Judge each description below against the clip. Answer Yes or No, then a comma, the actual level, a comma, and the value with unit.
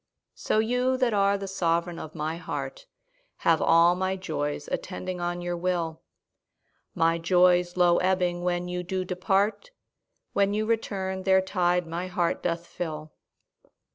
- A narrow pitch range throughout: Yes, narrow, 1.9 semitones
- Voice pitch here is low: No, medium, 180 Hz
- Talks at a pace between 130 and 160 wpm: Yes, average, 145 wpm